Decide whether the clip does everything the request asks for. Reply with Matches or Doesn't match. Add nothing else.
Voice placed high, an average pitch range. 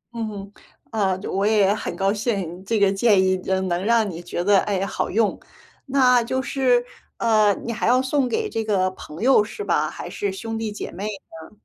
Matches